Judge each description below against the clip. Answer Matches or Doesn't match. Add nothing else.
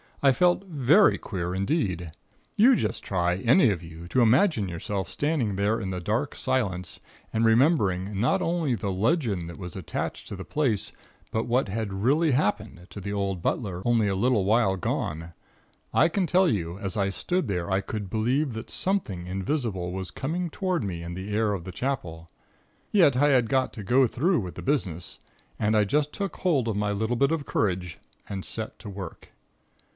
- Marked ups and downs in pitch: Matches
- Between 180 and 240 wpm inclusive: Matches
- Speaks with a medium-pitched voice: Doesn't match